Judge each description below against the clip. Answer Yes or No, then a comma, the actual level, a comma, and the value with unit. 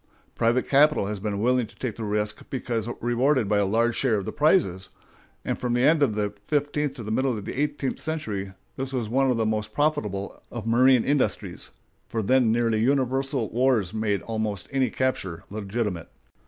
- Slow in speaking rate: No, average, 190 wpm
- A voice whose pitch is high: No, low, 120 Hz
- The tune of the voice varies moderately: Yes, average, 4.0 semitones